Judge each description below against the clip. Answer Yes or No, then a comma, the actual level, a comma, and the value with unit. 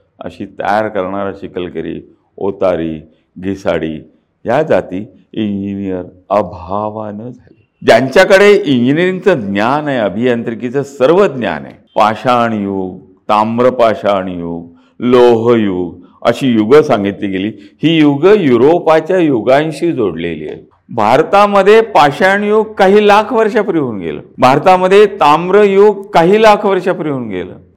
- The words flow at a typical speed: Yes, average, 110 wpm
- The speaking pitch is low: Yes, low, 125 Hz